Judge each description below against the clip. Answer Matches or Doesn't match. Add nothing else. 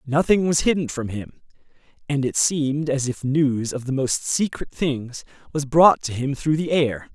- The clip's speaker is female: Doesn't match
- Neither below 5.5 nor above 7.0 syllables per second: Doesn't match